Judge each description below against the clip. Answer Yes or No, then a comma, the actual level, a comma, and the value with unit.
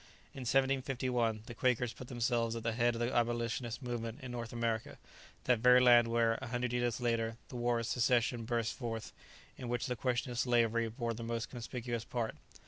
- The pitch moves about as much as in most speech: No, narrow, 1.2 semitones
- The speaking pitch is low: Yes, low, 120 Hz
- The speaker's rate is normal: Yes, average, 195 wpm